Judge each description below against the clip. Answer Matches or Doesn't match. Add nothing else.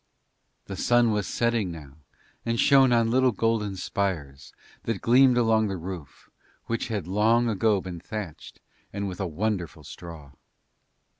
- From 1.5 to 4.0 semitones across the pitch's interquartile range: Doesn't match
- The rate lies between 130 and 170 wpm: Matches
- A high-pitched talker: Doesn't match